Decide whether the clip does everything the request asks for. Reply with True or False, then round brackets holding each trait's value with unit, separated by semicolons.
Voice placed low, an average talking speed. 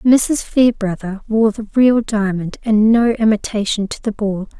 False (215 Hz; 155 wpm)